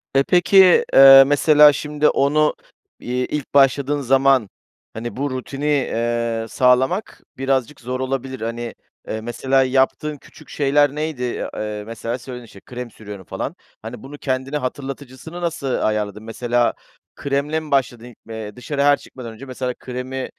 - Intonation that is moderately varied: Yes, average, 3.1 semitones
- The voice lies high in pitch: No, low, 130 Hz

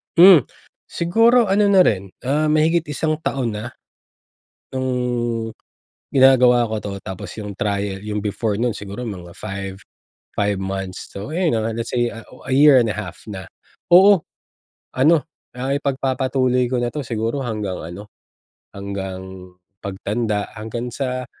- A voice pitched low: Yes, low, 120 Hz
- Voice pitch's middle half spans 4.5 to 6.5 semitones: Yes, average, 4.8 semitones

